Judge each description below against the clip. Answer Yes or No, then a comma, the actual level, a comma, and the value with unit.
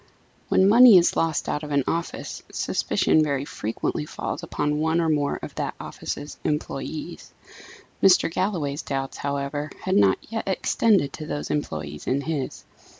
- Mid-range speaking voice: Yes, medium, 150 Hz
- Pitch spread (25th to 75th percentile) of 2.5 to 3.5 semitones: Yes, average, 3.2 semitones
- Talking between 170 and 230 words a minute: No, average, 150 wpm